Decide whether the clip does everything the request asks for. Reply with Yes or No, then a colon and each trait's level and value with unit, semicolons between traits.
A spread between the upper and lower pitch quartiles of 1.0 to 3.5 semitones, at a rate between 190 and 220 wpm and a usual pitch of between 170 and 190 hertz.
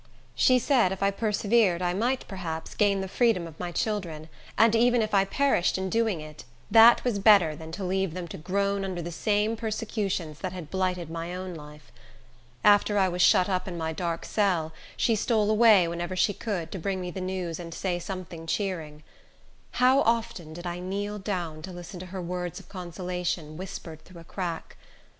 Yes: average, 3.2 semitones; average, 195 wpm; medium, 185 Hz